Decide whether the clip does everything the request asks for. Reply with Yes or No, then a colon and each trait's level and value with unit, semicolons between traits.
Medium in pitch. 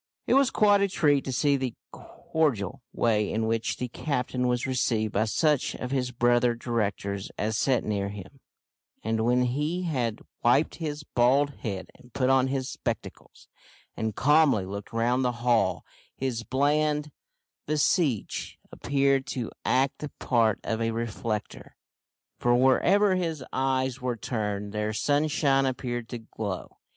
No: low, 125 Hz